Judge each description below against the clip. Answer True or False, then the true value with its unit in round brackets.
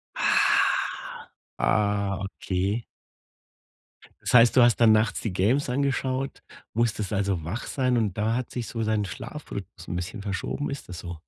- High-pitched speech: False (110 Hz)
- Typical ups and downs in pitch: True (3.8 semitones)